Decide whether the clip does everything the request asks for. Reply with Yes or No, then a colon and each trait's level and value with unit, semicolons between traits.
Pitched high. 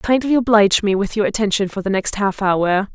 Yes: high, 205 Hz